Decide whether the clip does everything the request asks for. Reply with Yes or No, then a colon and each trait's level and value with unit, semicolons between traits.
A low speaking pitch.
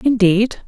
No: high, 220 Hz